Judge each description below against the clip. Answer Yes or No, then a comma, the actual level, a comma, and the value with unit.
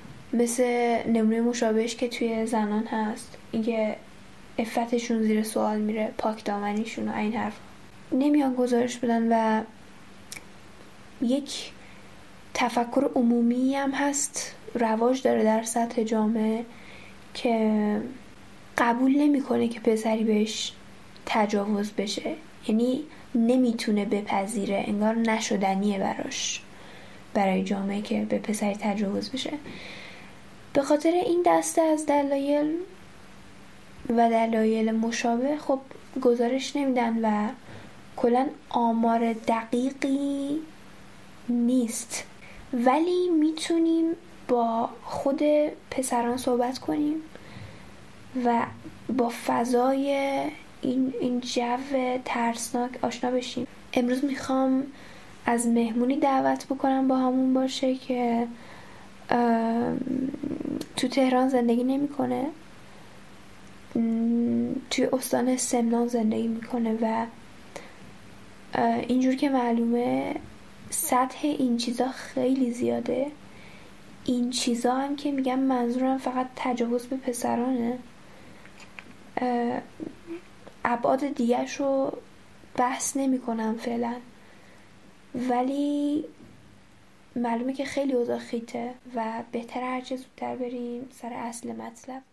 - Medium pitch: No, high, 245 Hz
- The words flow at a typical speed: No, slow, 95 wpm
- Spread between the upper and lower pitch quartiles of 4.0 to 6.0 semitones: No, narrow, 2.4 semitones